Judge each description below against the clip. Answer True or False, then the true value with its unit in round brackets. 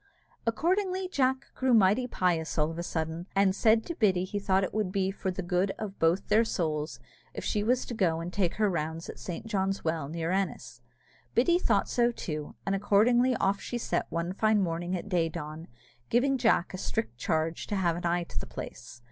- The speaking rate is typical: False (215 wpm)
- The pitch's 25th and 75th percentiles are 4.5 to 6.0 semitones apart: True (4.8 semitones)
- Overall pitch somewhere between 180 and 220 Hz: True (190 Hz)